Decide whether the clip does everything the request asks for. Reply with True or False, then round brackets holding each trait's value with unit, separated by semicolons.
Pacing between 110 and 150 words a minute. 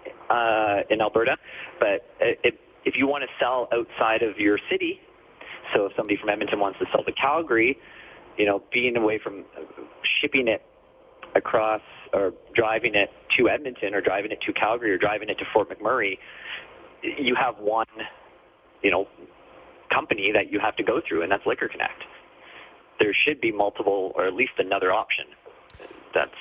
False (170 wpm)